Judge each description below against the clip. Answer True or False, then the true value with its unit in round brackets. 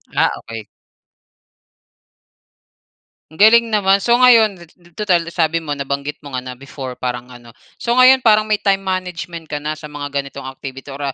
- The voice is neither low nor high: True (155 Hz)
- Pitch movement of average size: False (7.0 semitones)